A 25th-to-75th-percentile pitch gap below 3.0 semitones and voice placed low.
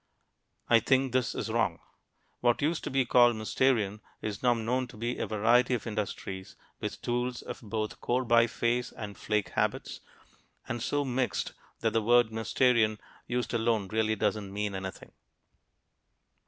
Yes: narrow, 2.4 semitones; low, 115 Hz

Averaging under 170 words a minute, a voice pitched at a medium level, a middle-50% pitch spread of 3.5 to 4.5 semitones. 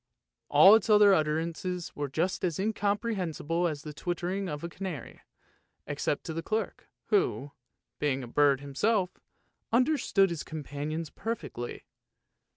No: average, 140 wpm; medium, 170 Hz; average, 5.1 semitones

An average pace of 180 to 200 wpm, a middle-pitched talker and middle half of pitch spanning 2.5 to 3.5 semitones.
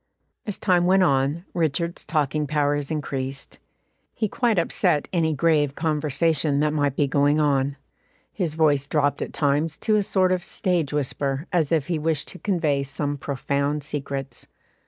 No: average, 155 wpm; medium, 150 Hz; average, 2.9 semitones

